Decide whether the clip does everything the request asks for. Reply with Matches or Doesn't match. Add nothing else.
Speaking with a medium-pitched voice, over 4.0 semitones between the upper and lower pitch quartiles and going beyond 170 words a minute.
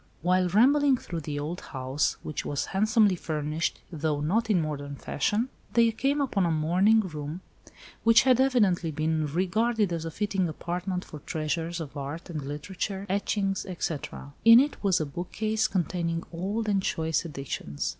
Doesn't match